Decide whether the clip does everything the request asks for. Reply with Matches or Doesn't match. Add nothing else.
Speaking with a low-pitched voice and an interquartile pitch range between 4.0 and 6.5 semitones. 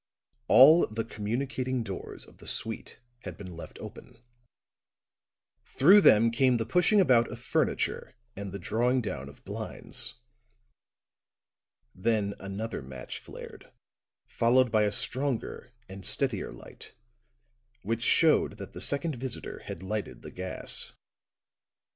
Matches